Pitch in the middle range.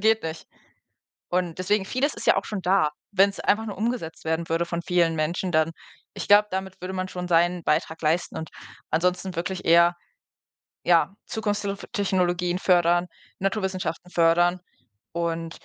Yes: medium, 180 Hz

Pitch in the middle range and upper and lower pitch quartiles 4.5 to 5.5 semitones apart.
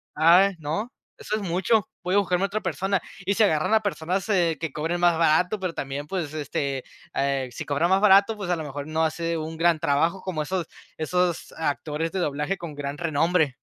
No: medium, 170 Hz; average, 3.8 semitones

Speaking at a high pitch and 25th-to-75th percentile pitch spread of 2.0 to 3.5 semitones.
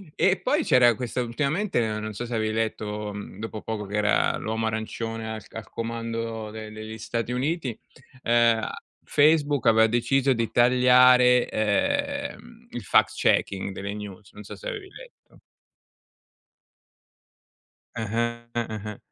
No: low, 115 Hz; average, 2.7 semitones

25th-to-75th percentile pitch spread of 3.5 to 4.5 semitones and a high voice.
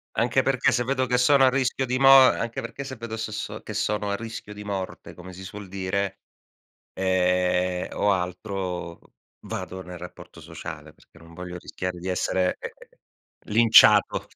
No: average, 4.2 semitones; low, 100 Hz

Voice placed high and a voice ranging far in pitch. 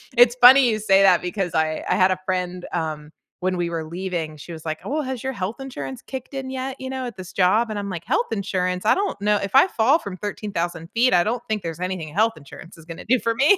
Yes: high, 195 Hz; wide, 5.7 semitones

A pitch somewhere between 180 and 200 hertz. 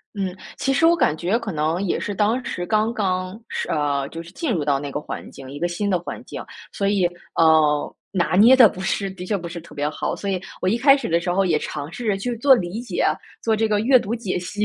Yes: medium, 185 Hz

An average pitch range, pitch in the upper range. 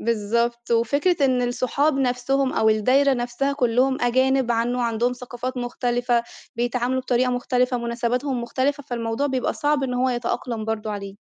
No: narrow, 1.8 semitones; high, 245 Hz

